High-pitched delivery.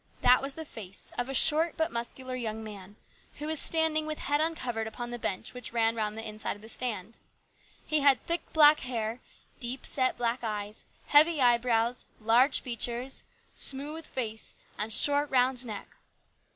Yes: high, 245 Hz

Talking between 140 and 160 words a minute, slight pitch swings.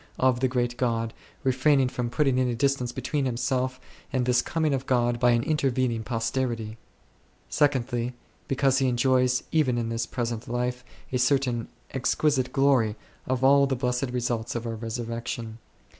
Yes: average, 155 wpm; narrow, 1.9 semitones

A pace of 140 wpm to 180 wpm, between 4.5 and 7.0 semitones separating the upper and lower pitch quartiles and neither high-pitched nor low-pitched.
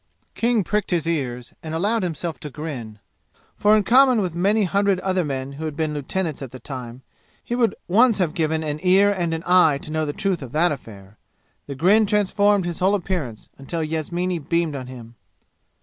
No: average, 195 wpm; average, 5.3 semitones; medium, 165 Hz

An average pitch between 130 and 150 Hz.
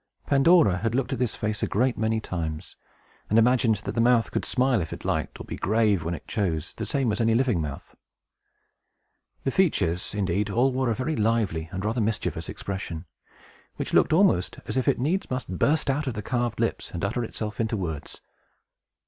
No: low, 110 Hz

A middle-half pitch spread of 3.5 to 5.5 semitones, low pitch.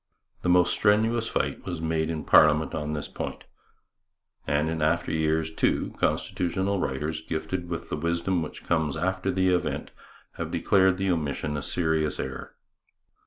No: average, 3.0 semitones; very low, 80 Hz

